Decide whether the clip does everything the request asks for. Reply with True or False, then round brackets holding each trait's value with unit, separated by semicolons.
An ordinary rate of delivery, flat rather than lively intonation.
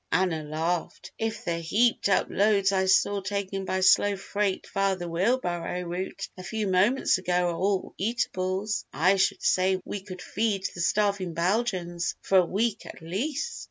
True (170 wpm; 2.3 semitones)